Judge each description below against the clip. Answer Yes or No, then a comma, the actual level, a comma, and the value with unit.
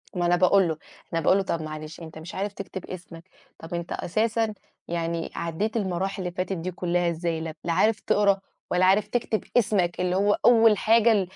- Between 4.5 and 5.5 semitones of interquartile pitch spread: No, average, 3.3 semitones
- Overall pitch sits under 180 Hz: No, medium, 185 Hz